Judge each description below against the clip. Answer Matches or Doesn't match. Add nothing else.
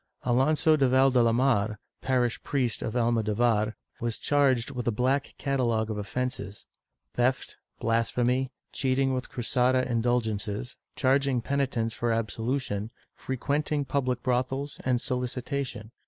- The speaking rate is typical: Doesn't match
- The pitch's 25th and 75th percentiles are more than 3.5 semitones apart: Doesn't match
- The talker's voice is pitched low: Matches